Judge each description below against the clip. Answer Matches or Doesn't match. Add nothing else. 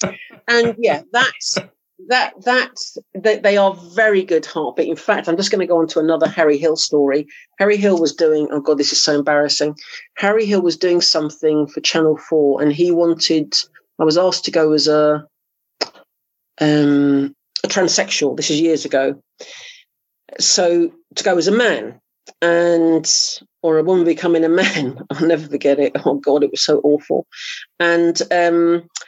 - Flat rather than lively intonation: Doesn't match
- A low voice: Doesn't match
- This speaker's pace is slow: Doesn't match